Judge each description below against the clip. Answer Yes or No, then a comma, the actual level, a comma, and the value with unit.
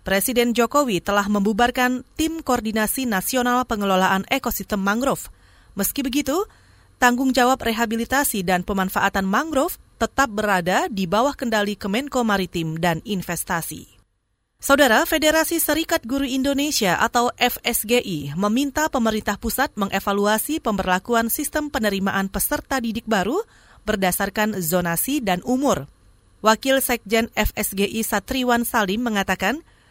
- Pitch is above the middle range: Yes, high, 225 Hz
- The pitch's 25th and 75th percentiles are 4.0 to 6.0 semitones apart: Yes, average, 5.2 semitones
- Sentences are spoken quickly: No, average, 110 wpm